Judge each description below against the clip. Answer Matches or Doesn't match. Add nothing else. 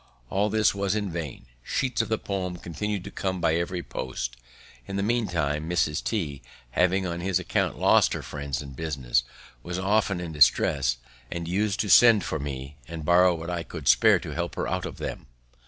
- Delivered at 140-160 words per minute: Doesn't match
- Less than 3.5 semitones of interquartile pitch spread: Doesn't match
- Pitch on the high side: Doesn't match